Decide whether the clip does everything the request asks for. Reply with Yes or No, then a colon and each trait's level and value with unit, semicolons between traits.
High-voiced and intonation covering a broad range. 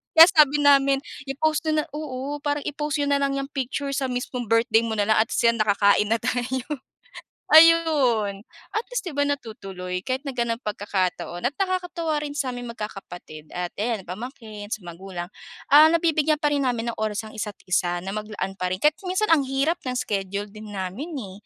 Yes: high, 245 Hz; wide, 6.0 semitones